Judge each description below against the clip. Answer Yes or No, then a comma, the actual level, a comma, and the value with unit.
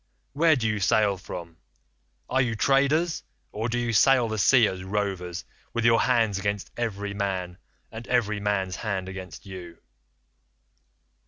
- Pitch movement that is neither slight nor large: Yes, average, 3.9 semitones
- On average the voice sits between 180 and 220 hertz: No, low, 105 Hz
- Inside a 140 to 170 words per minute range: Yes, average, 145 wpm